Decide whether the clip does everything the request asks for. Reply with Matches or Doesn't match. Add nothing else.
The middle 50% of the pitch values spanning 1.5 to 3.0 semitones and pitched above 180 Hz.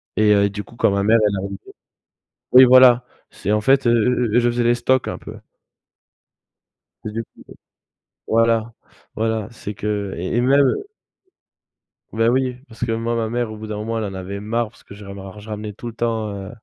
Doesn't match